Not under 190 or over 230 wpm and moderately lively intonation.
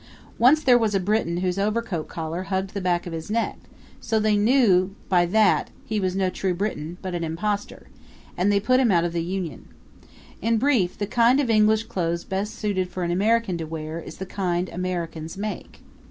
Yes: average, 200 wpm; average, 3.6 semitones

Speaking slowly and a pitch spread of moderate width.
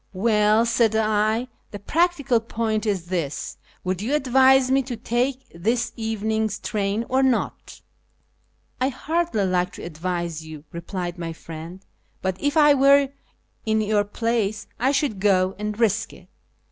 No: average, 165 wpm; average, 5.0 semitones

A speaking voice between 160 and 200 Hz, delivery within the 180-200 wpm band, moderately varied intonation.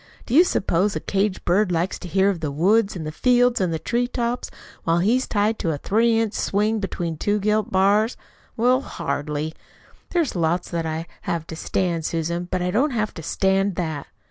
Yes: high, 190 Hz; average, 195 wpm; average, 4.7 semitones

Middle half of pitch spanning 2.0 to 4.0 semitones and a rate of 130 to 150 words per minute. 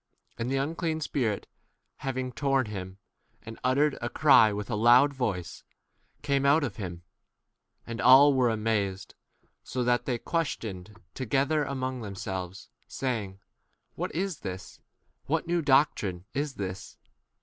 No: average, 5.2 semitones; average, 140 wpm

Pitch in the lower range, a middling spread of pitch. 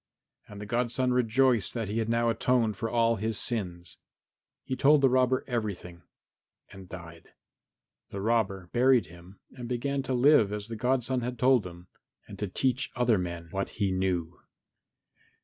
Yes: low, 115 Hz; average, 4.6 semitones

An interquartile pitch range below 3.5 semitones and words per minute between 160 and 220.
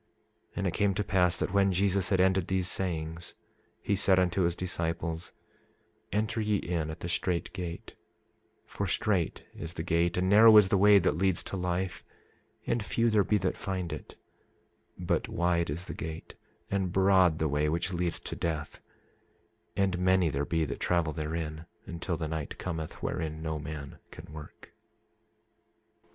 Yes: average, 2.9 semitones; average, 170 wpm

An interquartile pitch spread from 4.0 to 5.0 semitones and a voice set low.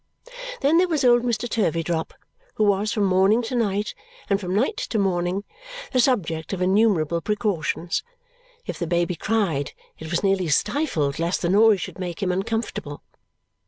No: average, 4.6 semitones; high, 195 Hz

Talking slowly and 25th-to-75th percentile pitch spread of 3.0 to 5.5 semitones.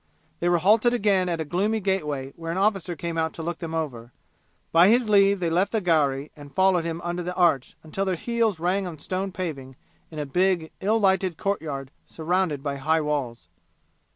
No: average, 200 wpm; average, 3.7 semitones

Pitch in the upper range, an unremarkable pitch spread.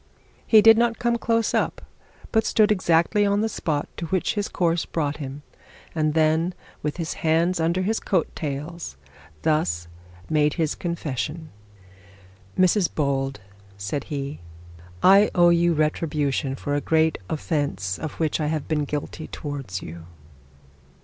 No: medium, 160 Hz; average, 3.5 semitones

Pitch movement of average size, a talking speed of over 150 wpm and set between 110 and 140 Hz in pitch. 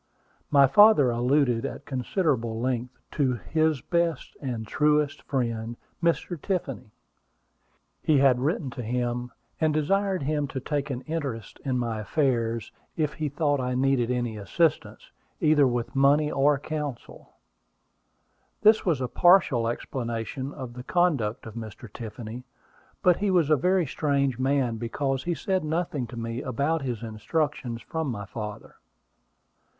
No: average, 4.4 semitones; average, 145 wpm; low, 135 Hz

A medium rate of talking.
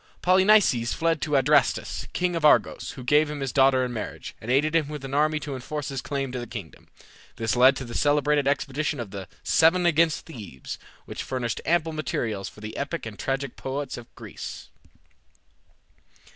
Yes: average, 185 wpm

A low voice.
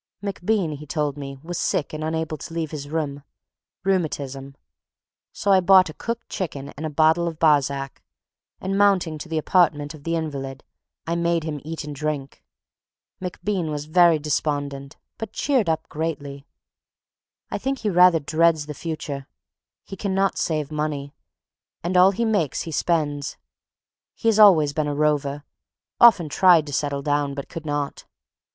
No: medium, 155 Hz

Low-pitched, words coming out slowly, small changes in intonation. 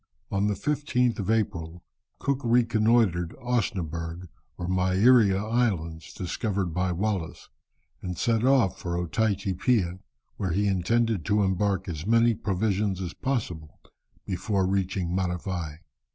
No: very low, 95 Hz; slow, 125 wpm; average, 4.1 semitones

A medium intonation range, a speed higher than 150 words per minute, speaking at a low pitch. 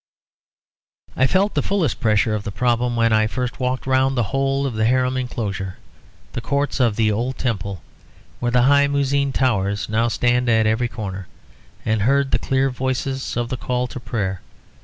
Yes: average, 3.2 semitones; average, 180 wpm; low, 125 Hz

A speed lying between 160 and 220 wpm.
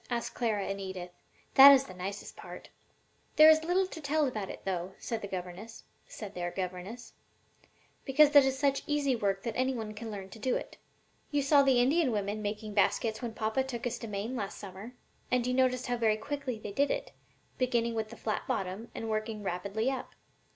Yes: average, 195 wpm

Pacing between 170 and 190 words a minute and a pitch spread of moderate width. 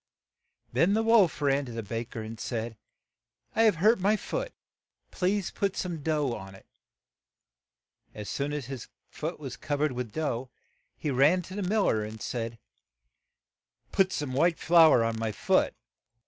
No: average, 175 wpm; wide, 7.7 semitones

